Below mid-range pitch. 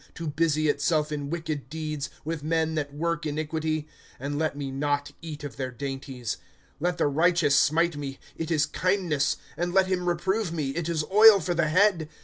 No: medium, 155 Hz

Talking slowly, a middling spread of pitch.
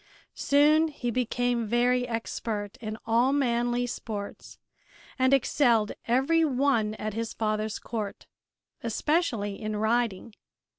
Yes: slow, 110 wpm; average, 3.0 semitones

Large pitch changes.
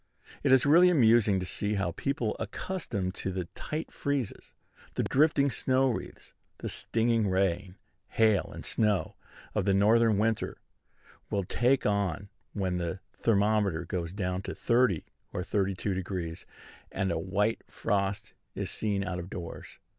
No: average, 3.7 semitones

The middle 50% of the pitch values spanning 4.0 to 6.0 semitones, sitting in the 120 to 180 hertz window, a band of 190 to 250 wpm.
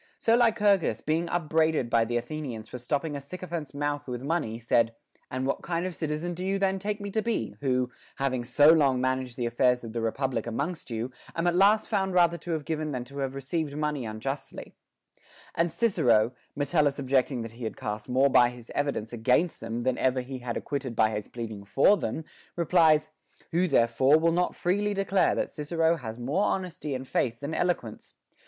Yes: wide, 5.5 semitones; medium, 140 Hz; average, 200 wpm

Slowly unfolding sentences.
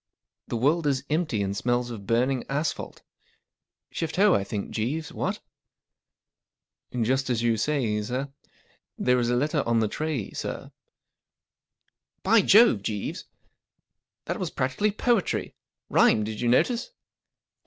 No: average, 145 wpm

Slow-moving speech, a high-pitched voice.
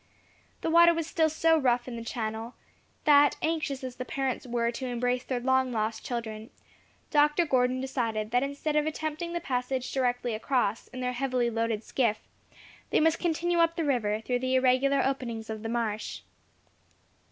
No: average, 175 wpm; very high, 255 Hz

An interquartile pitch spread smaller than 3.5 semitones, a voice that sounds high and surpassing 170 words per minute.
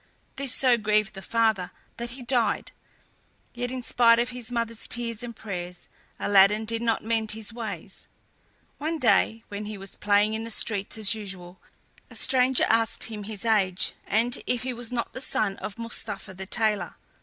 Yes: narrow, 2.6 semitones; high, 225 Hz; average, 180 wpm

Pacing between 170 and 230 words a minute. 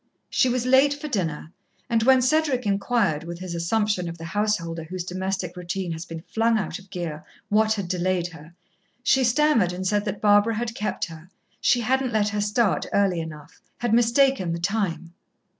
Yes: average, 185 wpm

